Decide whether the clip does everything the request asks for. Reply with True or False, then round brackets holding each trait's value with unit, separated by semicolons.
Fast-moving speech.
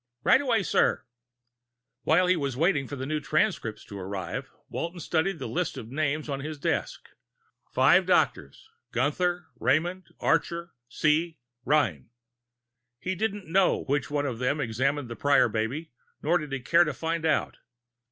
False (155 wpm)